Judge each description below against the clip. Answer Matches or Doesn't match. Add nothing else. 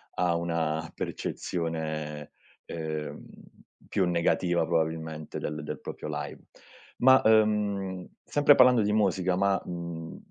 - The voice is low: Matches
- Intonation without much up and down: Doesn't match